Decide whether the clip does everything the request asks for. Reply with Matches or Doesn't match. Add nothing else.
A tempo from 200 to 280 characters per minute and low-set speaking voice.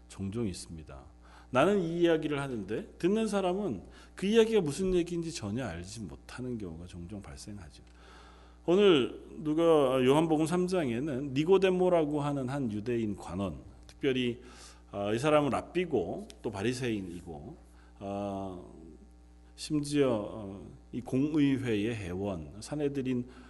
Matches